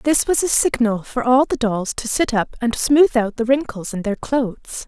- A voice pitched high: Yes, high, 240 Hz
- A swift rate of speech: Yes, fast, 235 wpm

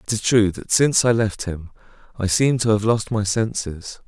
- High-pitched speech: No, low, 105 Hz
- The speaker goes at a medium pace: No, fast, 220 wpm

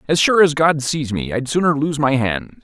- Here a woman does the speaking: No, male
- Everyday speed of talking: No, fast, 250 wpm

